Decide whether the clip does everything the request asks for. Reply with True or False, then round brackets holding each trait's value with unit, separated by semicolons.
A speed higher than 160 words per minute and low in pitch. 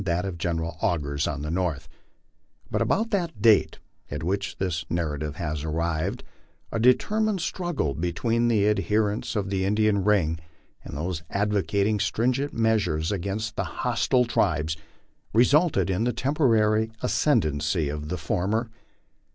False (145 wpm; 100 Hz)